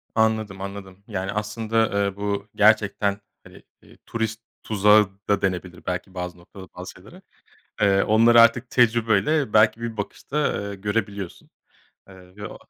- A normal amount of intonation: No, narrow, 2.3 semitones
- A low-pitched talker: Yes, low, 105 Hz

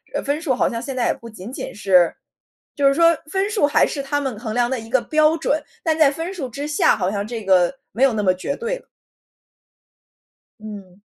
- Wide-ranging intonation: Yes, wide, 6.2 semitones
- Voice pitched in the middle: No, very high, 260 Hz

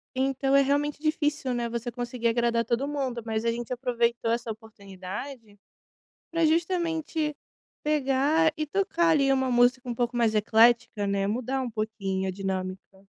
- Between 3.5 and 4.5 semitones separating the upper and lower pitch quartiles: Yes, average, 4.2 semitones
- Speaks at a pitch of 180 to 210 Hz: No, high, 240 Hz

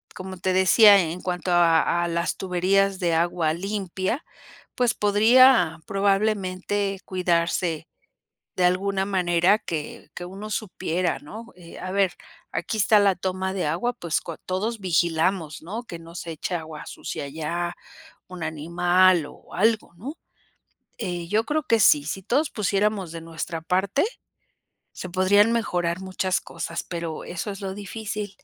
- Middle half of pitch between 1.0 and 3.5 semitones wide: Yes, average, 3.0 semitones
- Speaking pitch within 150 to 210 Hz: Yes, medium, 185 Hz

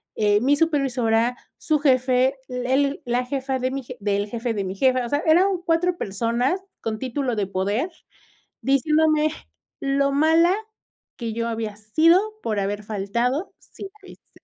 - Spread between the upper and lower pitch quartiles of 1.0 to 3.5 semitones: No, average, 4.4 semitones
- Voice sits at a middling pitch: No, very high, 255 Hz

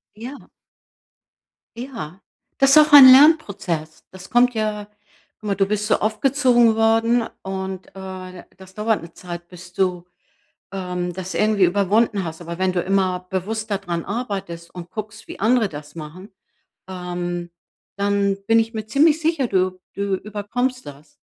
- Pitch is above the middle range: Yes, high, 200 Hz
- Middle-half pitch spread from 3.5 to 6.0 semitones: Yes, average, 3.8 semitones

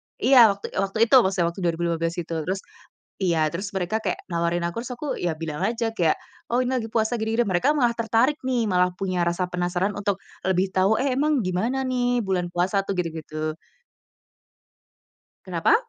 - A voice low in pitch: No, high, 195 Hz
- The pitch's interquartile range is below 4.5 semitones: No, average, 4.8 semitones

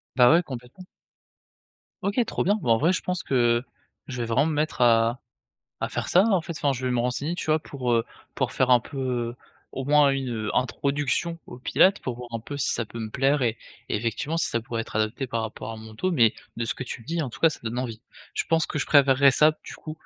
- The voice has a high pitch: No, low, 130 Hz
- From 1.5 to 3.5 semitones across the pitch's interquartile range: No, average, 4.3 semitones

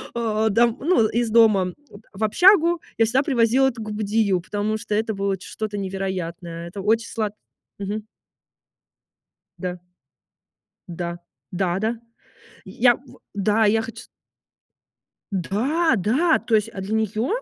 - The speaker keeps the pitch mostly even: No, average, 3.0 semitones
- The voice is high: Yes, high, 215 Hz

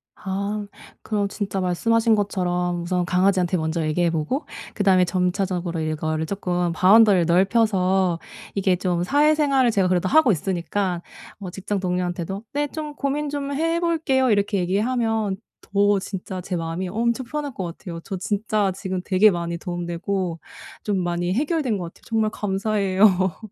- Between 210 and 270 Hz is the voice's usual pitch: No, high, 195 Hz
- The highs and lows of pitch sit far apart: No, average, 3.6 semitones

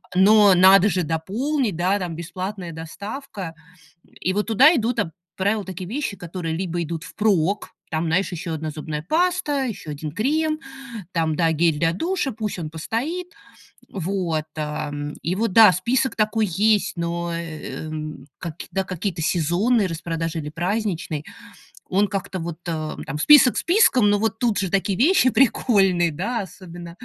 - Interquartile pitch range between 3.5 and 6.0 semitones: Yes, average, 4.9 semitones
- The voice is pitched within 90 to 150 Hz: No, medium, 185 Hz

